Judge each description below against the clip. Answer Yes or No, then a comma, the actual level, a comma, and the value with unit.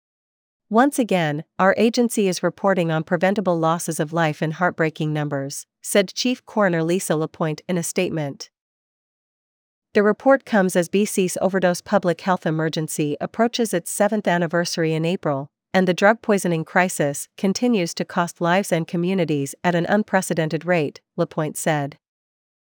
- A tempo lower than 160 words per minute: Yes, average, 145 wpm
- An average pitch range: Yes, average, 3.4 semitones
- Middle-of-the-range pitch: Yes, medium, 175 Hz